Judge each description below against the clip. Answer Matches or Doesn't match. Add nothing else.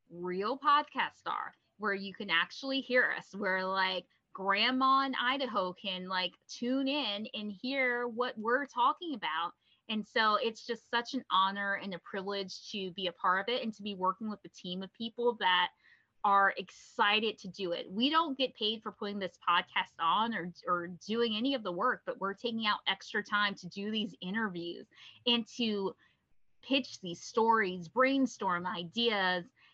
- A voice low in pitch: Doesn't match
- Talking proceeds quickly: Doesn't match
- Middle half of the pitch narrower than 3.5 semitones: Doesn't match